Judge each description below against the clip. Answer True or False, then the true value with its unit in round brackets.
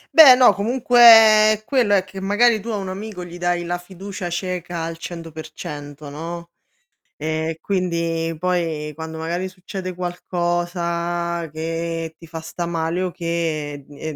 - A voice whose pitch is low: False (175 Hz)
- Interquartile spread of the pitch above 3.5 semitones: False (2.4 semitones)